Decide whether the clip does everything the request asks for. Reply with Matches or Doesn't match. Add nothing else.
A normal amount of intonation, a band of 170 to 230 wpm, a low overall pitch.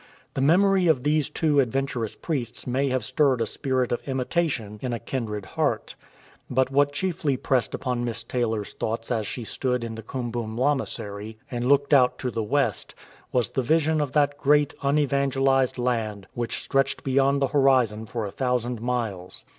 Matches